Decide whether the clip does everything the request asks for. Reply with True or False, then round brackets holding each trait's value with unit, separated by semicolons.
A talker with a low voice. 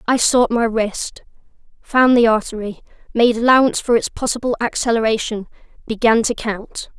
False (230 Hz)